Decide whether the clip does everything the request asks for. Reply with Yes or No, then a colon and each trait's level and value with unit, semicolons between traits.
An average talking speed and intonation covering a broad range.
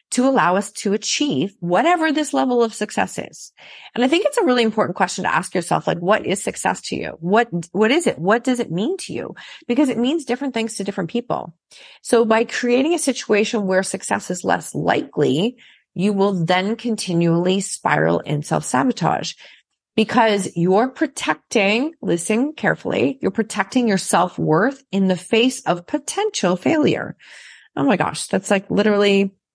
No: average, 170 wpm; average, 4.8 semitones